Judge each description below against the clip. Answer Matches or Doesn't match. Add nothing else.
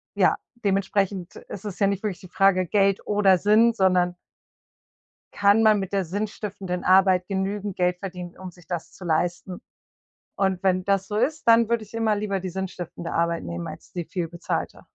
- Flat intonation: Matches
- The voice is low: Doesn't match